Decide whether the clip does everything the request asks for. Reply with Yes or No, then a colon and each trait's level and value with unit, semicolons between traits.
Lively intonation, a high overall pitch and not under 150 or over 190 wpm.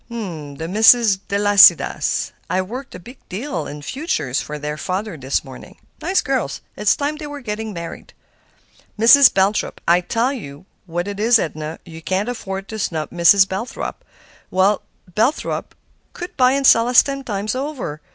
Yes: wide, 6.4 semitones; high, 205 Hz; average, 160 wpm